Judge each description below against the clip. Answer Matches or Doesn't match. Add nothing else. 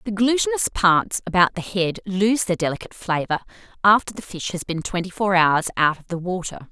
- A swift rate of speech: Doesn't match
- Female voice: Matches